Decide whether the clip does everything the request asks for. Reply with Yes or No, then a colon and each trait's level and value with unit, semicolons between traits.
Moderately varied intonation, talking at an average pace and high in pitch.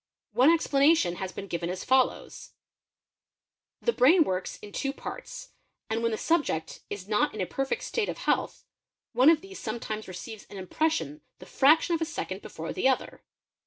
No: wide, 8.3 semitones; average, 170 wpm; very high, 255 Hz